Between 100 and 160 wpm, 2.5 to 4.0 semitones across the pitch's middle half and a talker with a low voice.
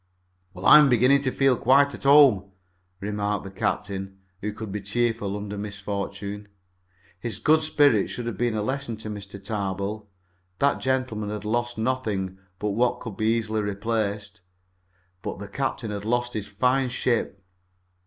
Yes: average, 155 wpm; average, 3.2 semitones; low, 110 Hz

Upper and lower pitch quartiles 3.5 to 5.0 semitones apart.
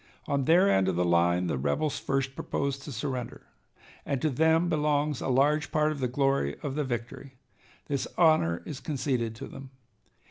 Yes: average, 4.2 semitones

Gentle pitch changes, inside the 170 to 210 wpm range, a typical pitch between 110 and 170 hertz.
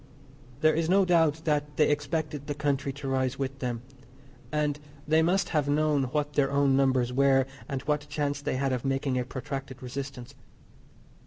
Yes: narrow, 2.0 semitones; average, 175 wpm; medium, 140 Hz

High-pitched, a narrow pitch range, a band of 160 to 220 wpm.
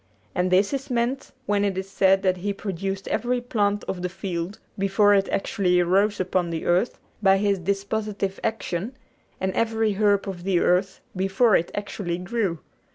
Yes: high, 195 Hz; narrow, 2.1 semitones; average, 170 wpm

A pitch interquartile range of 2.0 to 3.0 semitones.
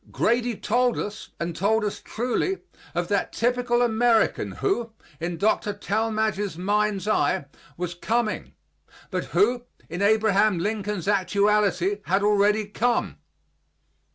Yes: narrow, 2.4 semitones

